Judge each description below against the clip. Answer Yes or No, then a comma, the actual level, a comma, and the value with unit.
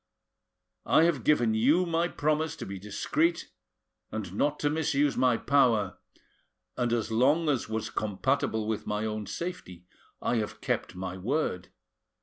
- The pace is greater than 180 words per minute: No, average, 145 wpm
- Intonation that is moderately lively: No, wide, 6.0 semitones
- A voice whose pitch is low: Yes, low, 120 Hz